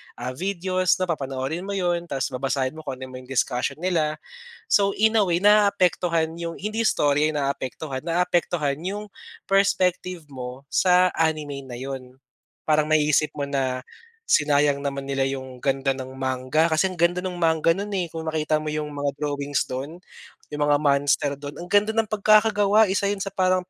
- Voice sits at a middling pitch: Yes, medium, 155 Hz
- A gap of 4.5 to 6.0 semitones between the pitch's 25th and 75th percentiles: Yes, average, 4.9 semitones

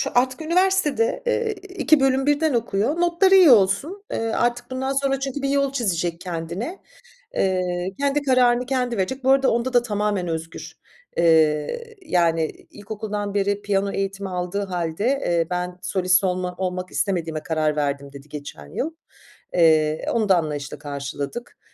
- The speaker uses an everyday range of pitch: No, wide, 7.7 semitones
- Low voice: No, high, 200 Hz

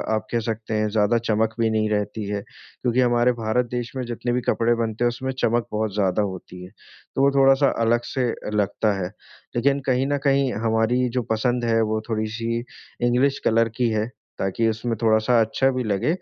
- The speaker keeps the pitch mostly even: Yes, narrow, 2.3 semitones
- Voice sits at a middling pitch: No, low, 115 Hz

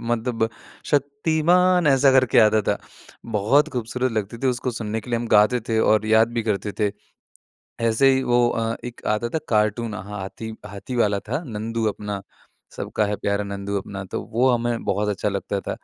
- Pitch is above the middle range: No, low, 115 Hz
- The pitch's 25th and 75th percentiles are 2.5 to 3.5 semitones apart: Yes, average, 3.0 semitones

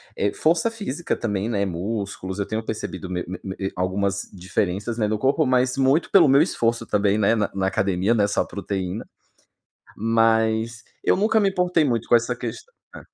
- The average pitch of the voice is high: No, low, 110 Hz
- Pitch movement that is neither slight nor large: Yes, average, 4.7 semitones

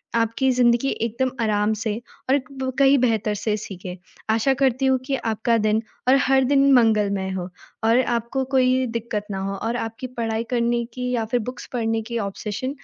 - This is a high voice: Yes, high, 235 Hz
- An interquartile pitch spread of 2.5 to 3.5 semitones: Yes, average, 2.9 semitones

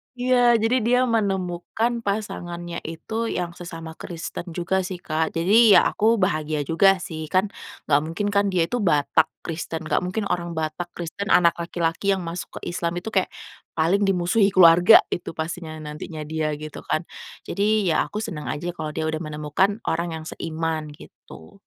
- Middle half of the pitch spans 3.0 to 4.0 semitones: Yes, average, 3.7 semitones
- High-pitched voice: No, medium, 175 Hz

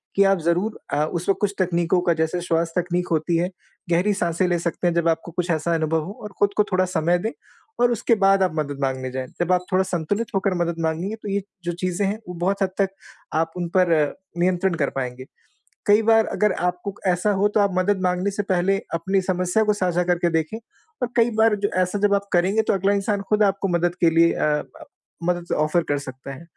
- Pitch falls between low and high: Yes, medium, 180 Hz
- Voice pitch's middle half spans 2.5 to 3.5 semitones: Yes, average, 2.9 semitones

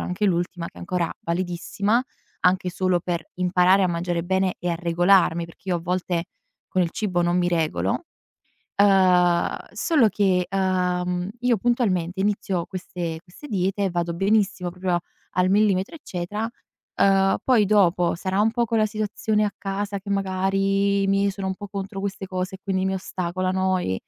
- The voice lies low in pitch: No, medium, 185 Hz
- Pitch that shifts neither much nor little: No, narrow, 2.0 semitones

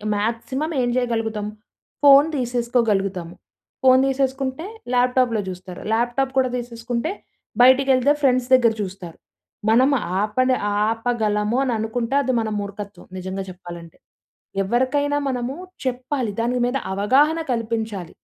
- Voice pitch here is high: Yes, high, 240 Hz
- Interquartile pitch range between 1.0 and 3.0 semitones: No, average, 3.6 semitones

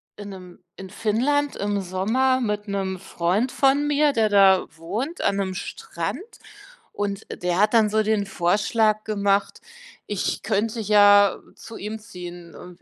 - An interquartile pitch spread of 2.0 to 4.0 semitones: Yes, narrow, 2.6 semitones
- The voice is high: Yes, high, 205 Hz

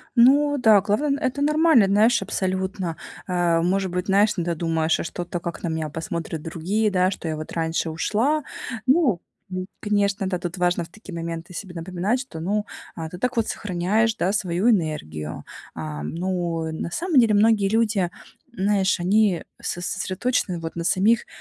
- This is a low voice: No, medium, 185 Hz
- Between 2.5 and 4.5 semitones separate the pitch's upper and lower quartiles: Yes, average, 4.2 semitones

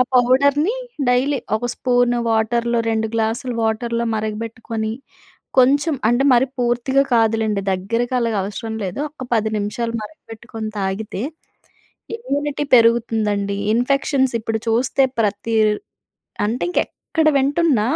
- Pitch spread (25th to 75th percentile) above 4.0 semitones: No, average, 2.8 semitones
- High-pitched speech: Yes, high, 235 Hz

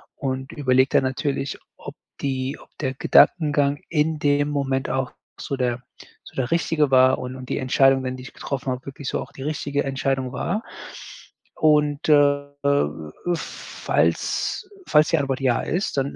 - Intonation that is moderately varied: No, narrow, 1.9 semitones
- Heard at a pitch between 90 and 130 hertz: No, medium, 140 Hz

